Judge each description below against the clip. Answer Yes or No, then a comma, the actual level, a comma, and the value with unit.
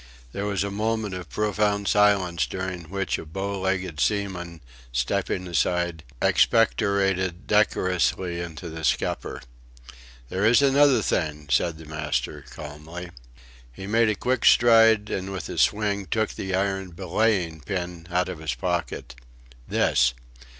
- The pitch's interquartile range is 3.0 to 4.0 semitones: Yes, average, 3.3 semitones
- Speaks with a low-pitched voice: Yes, very low, 95 Hz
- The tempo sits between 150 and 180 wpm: No, slow, 135 wpm